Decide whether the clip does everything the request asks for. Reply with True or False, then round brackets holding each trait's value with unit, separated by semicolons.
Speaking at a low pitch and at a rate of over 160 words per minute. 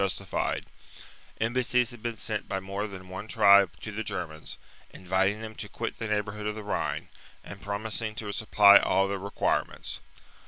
True (105 Hz; 170 wpm)